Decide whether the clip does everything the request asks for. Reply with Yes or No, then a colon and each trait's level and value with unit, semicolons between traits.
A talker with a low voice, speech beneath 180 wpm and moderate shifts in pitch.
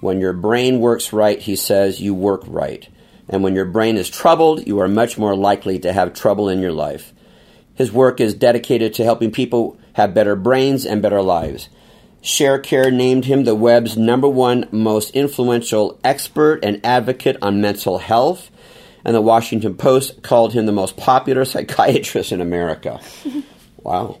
Yes: low, 115 Hz; average, 170 wpm; average, 4.2 semitones